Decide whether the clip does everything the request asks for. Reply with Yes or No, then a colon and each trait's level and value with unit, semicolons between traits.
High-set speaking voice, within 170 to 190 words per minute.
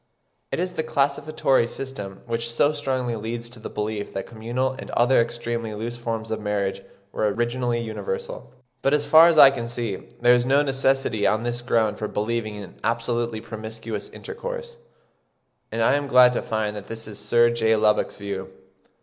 No: low, 120 Hz; average, 180 wpm